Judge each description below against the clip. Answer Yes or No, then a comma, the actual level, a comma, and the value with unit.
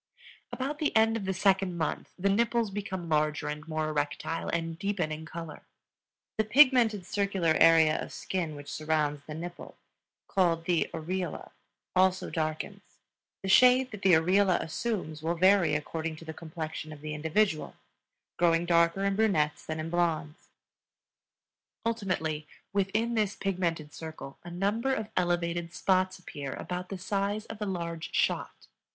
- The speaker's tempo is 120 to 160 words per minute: Yes, average, 150 wpm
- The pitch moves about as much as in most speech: Yes, average, 3.9 semitones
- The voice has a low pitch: No, medium, 175 Hz